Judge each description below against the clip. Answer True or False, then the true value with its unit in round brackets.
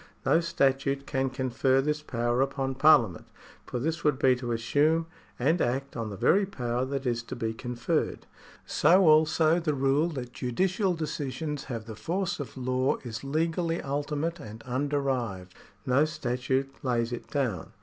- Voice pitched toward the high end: False (135 Hz)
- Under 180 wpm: True (160 wpm)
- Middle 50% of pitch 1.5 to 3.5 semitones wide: False (3.9 semitones)